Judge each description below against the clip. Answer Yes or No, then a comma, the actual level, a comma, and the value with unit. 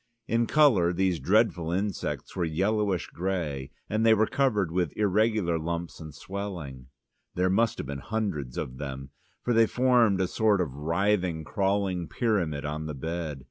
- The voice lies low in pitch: Yes, very low, 90 Hz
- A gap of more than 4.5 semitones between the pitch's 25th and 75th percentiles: Yes, average, 5.2 semitones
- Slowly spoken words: No, average, 160 wpm